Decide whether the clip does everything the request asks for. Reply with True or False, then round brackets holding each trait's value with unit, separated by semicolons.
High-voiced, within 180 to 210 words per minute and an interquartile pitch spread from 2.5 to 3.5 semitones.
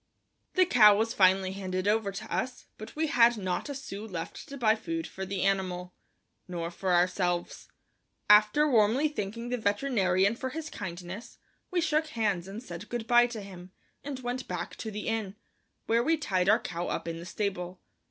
False (210 Hz; 185 wpm; 4.5 semitones)